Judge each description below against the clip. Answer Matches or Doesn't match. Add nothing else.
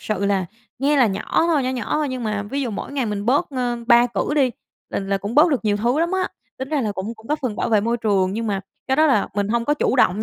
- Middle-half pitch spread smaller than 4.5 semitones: Doesn't match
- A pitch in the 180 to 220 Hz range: Doesn't match